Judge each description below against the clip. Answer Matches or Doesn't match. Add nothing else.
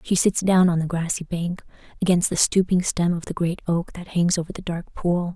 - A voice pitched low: Doesn't match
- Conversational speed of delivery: Doesn't match